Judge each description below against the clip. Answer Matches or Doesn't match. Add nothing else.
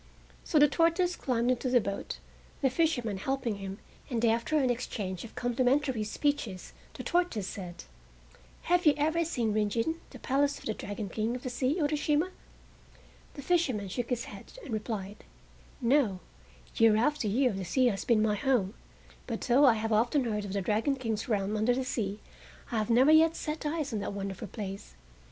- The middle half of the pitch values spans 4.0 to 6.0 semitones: Matches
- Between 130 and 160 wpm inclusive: Doesn't match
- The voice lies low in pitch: Doesn't match